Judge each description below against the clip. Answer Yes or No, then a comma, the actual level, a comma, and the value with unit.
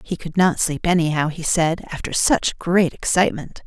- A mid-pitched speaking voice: Yes, medium, 170 Hz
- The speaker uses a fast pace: No, average, 180 wpm